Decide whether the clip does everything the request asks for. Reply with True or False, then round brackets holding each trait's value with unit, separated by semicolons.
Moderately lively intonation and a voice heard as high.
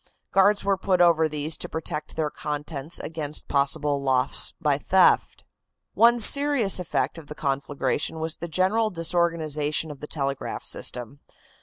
False (3.7 semitones; 160 Hz)